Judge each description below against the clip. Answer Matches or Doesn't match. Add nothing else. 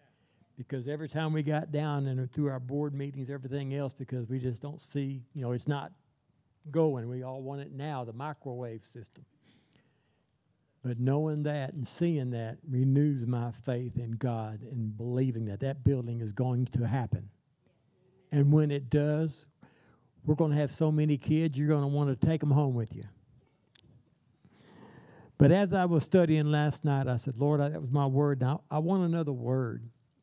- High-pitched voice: Doesn't match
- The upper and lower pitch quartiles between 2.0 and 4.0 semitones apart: Matches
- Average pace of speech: Matches